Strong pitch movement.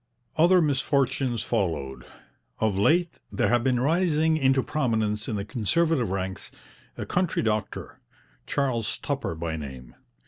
Yes: wide, 6.5 semitones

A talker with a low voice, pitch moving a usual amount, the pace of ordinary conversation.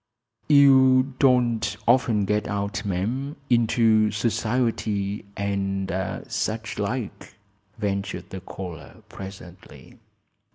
No: low, 105 Hz; average, 3.4 semitones; slow, 85 wpm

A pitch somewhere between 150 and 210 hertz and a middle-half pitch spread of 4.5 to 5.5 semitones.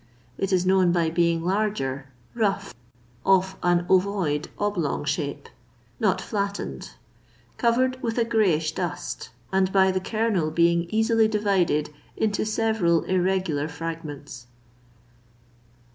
No: medium, 185 Hz; average, 4.0 semitones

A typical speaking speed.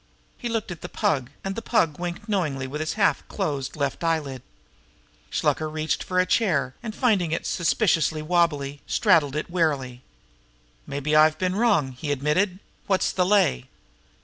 Yes: average, 170 wpm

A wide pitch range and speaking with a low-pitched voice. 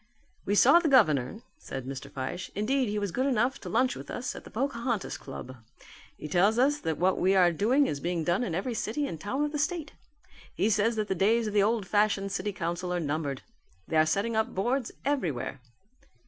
No: wide, 6.3 semitones; high, 205 Hz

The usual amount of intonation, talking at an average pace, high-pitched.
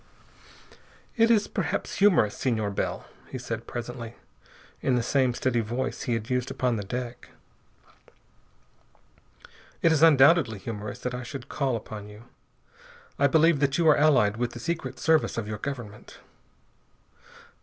No: average, 3.9 semitones; average, 145 wpm; low, 125 Hz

